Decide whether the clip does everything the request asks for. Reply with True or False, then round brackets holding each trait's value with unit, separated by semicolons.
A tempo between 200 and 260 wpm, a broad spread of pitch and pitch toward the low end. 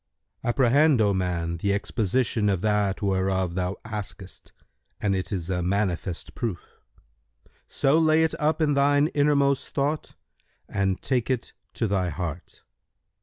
False (135 wpm; 6.8 semitones; 105 Hz)